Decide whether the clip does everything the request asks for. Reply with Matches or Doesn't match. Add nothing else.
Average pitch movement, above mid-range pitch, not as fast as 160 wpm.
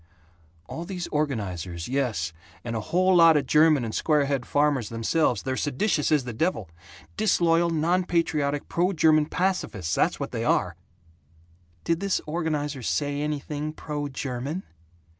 Doesn't match